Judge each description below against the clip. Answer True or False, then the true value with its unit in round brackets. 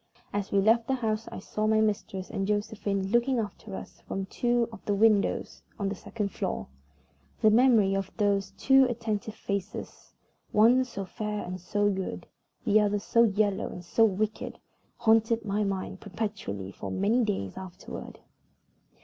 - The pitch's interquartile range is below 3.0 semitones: True (2.4 semitones)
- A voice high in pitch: True (210 Hz)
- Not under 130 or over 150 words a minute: False (160 wpm)